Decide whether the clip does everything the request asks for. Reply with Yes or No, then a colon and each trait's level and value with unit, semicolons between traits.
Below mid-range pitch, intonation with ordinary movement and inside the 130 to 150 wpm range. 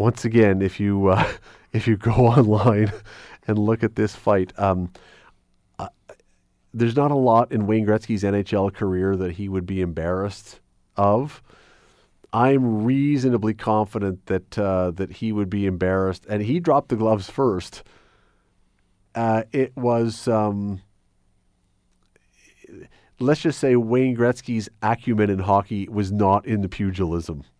Yes: low, 105 Hz; average, 3.2 semitones; average, 140 wpm